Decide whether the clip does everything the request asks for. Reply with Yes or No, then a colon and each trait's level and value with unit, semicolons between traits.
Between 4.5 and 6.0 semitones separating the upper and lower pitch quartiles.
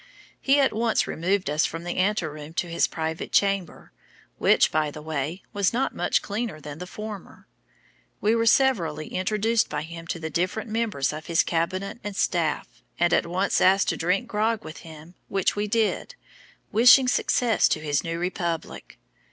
Yes: average, 4.9 semitones